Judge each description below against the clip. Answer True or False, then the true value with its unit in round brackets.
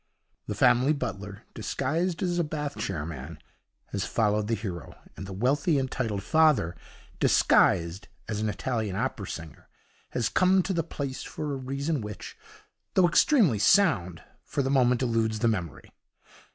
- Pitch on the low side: True (120 Hz)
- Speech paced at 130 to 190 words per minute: True (155 wpm)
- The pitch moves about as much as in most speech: False (6.9 semitones)